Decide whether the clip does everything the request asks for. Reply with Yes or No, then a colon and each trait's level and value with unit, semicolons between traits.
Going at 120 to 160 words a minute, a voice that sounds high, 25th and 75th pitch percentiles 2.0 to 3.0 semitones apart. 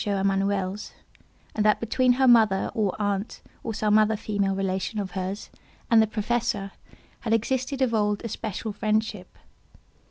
Yes: average, 150 wpm; high, 210 Hz; narrow, 2.4 semitones